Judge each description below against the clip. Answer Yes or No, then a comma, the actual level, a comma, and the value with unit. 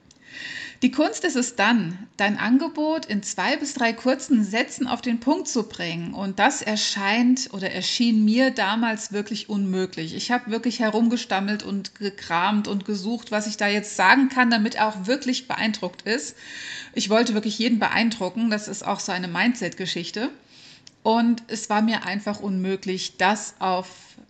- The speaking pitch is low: No, high, 215 Hz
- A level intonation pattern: No, average, 3.4 semitones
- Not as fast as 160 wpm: No, average, 165 wpm